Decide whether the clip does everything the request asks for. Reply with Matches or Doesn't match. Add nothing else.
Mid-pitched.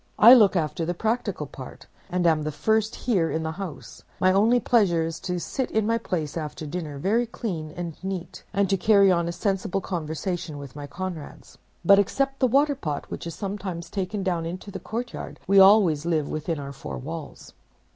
Matches